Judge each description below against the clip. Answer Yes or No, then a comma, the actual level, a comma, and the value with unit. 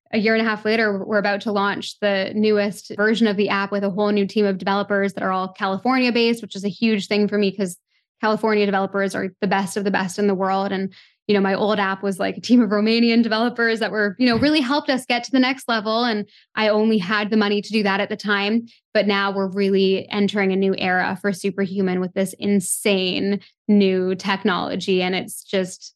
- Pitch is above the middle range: Yes, high, 205 Hz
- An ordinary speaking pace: No, fast, 235 wpm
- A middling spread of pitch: No, narrow, 1.8 semitones